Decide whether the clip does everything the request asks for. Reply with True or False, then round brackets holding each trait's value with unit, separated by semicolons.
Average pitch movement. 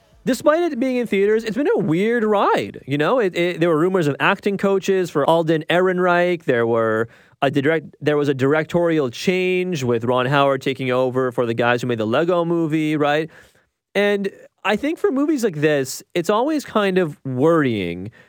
False (6.0 semitones)